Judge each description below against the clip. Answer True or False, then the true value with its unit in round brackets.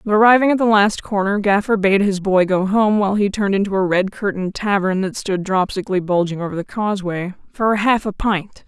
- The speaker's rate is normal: False (220 wpm)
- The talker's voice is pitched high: True (200 Hz)